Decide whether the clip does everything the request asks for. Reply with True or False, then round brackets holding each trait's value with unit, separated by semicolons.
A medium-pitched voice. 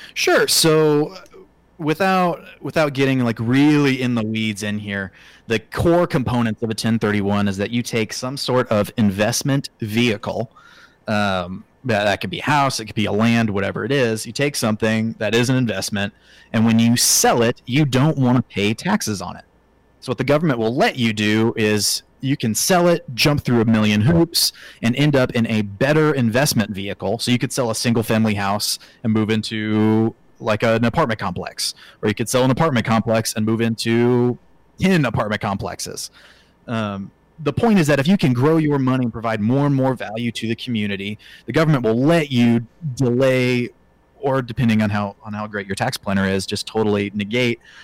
False (115 Hz)